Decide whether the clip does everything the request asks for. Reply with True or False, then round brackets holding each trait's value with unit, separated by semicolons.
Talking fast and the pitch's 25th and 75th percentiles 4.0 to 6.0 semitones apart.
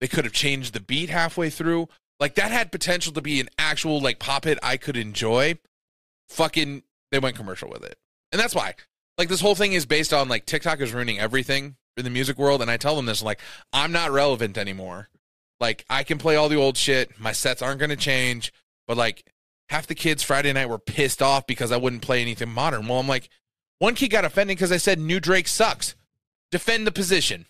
True (225 wpm; 4.7 semitones)